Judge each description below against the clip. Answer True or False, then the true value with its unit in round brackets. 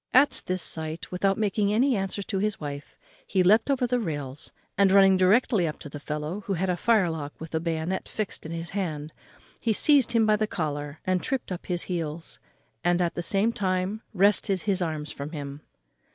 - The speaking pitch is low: False (185 Hz)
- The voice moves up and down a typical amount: True (4.6 semitones)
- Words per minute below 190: False (200 wpm)